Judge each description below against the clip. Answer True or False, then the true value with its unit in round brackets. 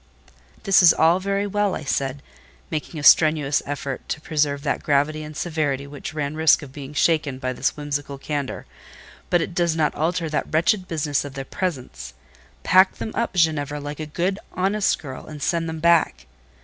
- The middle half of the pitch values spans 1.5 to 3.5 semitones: True (3.1 semitones)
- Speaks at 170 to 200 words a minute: True (185 wpm)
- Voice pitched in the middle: True (155 Hz)